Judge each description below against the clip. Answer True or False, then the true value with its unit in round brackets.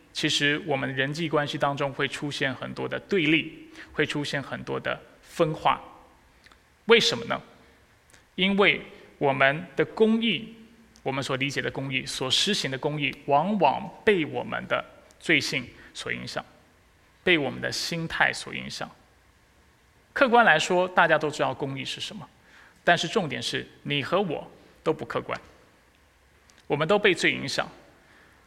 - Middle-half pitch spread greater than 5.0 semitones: True (5.4 semitones)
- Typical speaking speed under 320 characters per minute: True (220 characters per minute)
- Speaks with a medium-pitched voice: True (150 Hz)